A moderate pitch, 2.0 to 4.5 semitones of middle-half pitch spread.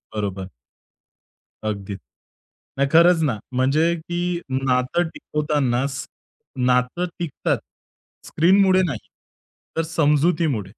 No: medium, 145 Hz; average, 5.0 semitones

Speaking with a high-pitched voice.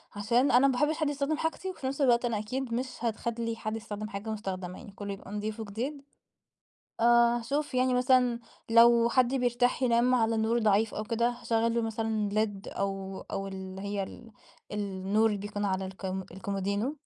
Yes: high, 225 Hz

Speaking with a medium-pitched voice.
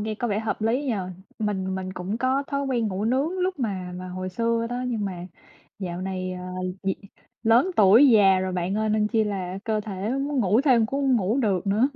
No: high, 215 Hz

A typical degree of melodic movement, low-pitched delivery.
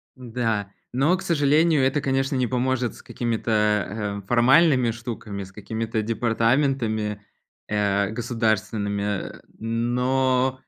Yes: average, 3.6 semitones; low, 115 Hz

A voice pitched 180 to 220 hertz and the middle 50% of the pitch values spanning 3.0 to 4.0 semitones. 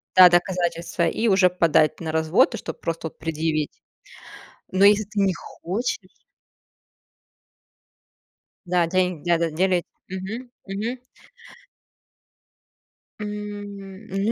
Yes: medium, 185 Hz; average, 3.3 semitones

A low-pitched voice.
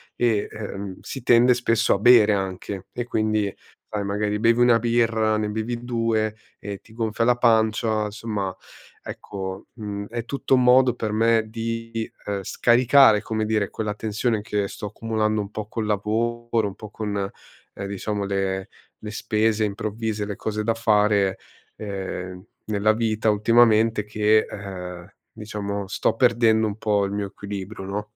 Yes: low, 110 Hz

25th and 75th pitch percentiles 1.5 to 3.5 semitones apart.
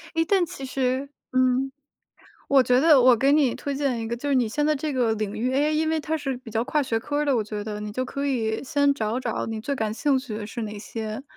No: average, 4.1 semitones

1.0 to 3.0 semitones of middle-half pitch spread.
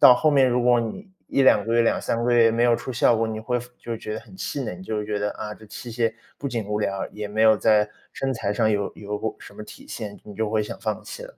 Yes: narrow, 2.4 semitones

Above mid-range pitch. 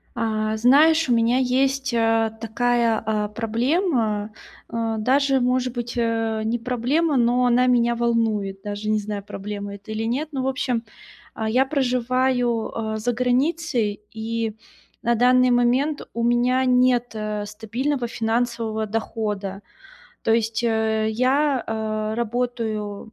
Yes: high, 235 Hz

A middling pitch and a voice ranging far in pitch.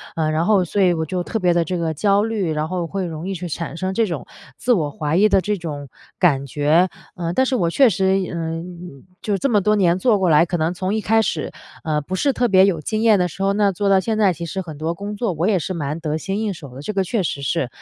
No: medium, 180 Hz; average, 3.8 semitones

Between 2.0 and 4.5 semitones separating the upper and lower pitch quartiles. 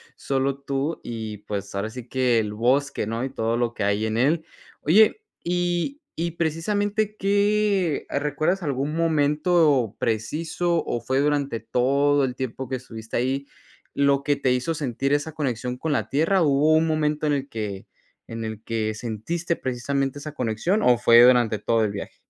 No: average, 5.2 semitones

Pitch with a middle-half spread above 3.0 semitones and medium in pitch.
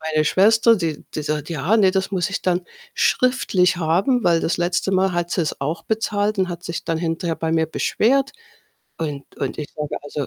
Yes: average, 3.4 semitones; medium, 175 Hz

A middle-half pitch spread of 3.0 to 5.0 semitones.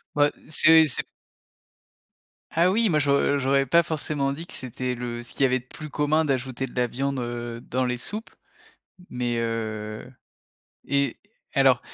Yes: average, 3.5 semitones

